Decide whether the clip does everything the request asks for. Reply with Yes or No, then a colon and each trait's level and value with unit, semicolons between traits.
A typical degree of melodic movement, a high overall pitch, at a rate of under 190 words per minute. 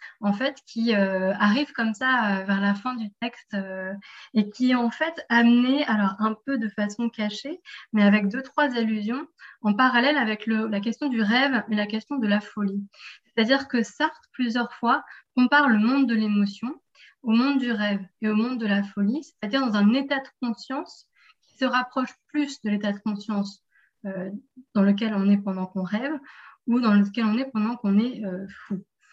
No: average, 4.0 semitones; high, 225 Hz; average, 200 wpm